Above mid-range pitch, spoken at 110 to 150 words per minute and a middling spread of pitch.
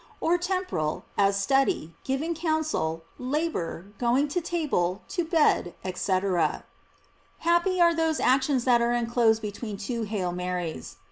No: high, 245 Hz; slow, 135 wpm; wide, 8.4 semitones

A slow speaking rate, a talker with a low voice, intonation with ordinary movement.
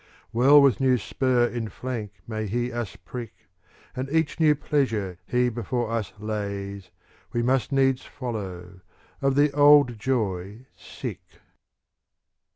Yes: slow, 130 wpm; low, 120 Hz; average, 4.2 semitones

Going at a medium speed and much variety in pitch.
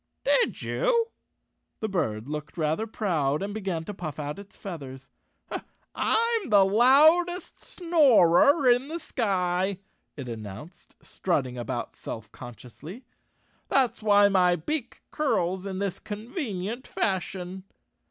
No: slow, 130 wpm; wide, 7.6 semitones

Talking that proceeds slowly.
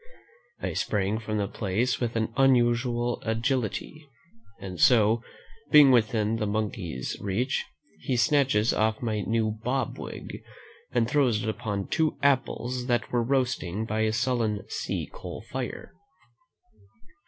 Yes: slow, 130 wpm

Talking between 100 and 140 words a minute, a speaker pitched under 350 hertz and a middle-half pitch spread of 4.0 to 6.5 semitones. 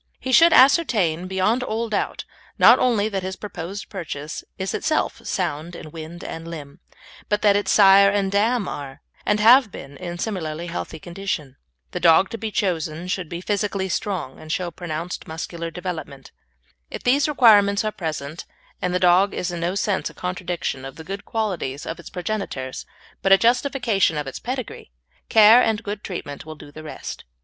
No: average, 180 wpm; medium, 185 Hz; average, 4.5 semitones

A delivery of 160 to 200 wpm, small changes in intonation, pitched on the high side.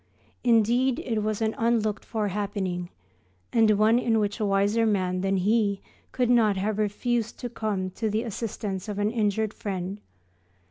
Yes: average, 165 wpm; narrow, 2.2 semitones; high, 215 Hz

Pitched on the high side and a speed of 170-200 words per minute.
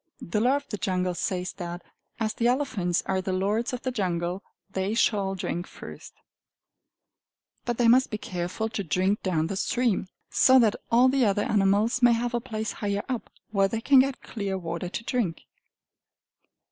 Yes: high, 205 Hz; average, 180 wpm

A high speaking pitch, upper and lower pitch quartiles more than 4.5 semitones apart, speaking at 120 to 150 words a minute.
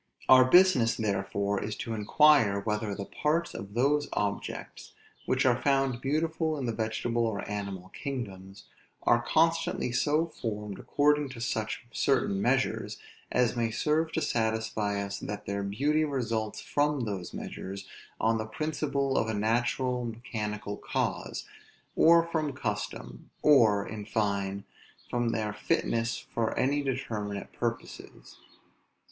No: low, 115 Hz; average, 5.0 semitones; slow, 135 wpm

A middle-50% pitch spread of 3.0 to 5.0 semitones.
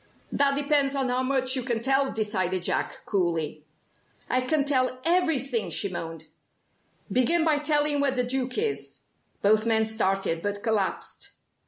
No: wide, 5.5 semitones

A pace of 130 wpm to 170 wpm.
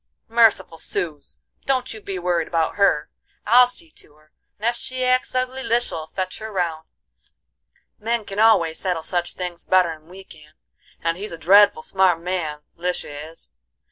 Yes: average, 165 wpm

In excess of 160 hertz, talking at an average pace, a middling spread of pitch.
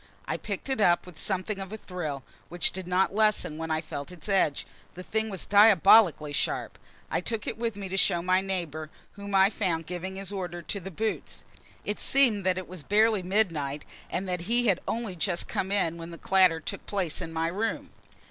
No: medium, 185 Hz; fast, 210 wpm; average, 3.2 semitones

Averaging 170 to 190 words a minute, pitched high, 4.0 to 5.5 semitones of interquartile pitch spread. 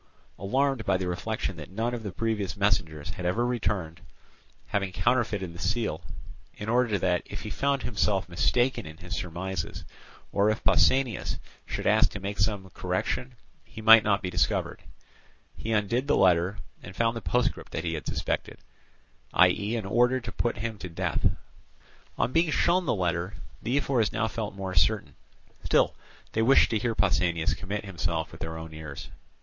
No: average, 175 wpm; low, 100 Hz; average, 4.4 semitones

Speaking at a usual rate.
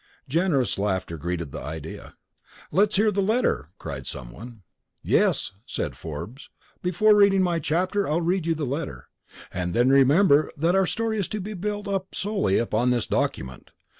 Yes: average, 165 wpm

